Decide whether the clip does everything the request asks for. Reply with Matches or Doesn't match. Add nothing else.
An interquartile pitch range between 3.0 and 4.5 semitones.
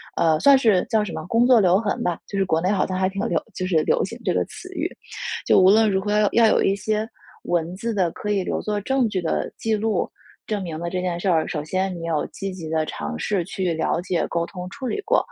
Matches